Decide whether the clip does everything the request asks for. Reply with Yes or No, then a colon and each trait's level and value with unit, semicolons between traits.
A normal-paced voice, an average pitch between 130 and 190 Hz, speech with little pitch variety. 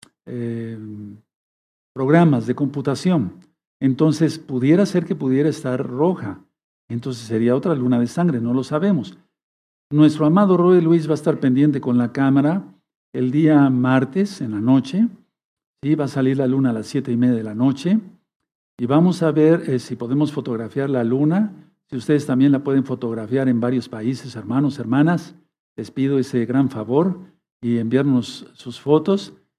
No: average, 165 wpm; low, 135 Hz; average, 3.9 semitones